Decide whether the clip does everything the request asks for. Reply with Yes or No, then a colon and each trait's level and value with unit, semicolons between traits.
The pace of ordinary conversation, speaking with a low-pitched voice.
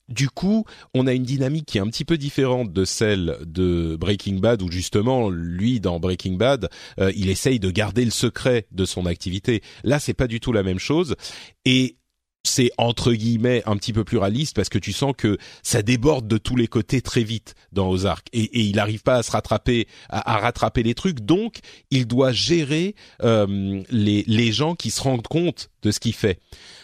Yes: average, 210 wpm; low, 115 Hz